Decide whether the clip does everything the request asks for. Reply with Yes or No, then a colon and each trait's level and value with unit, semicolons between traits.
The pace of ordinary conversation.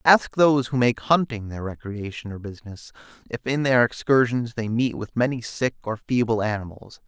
Yes: average, 180 wpm